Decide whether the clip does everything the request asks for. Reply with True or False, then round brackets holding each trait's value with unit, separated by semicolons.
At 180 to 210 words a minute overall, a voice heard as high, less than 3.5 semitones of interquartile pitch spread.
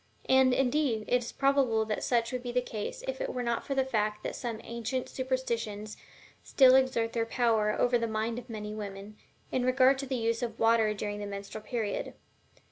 True (200 wpm; 235 Hz; 3.0 semitones)